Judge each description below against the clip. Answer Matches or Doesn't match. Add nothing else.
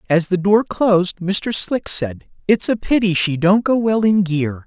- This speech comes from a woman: Doesn't match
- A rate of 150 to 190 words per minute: Doesn't match